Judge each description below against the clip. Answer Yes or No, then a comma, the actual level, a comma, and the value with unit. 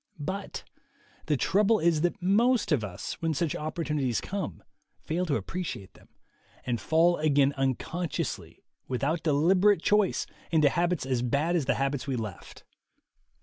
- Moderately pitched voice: Yes, medium, 155 Hz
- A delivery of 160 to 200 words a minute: No, average, 145 wpm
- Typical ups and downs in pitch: Yes, average, 4.5 semitones